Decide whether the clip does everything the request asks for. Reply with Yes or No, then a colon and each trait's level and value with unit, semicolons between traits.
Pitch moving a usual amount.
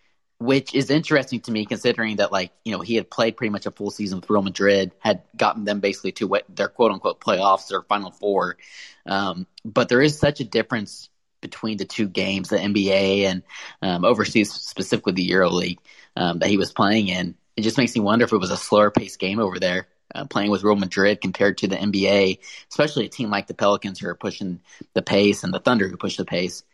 No: narrow, 2.0 semitones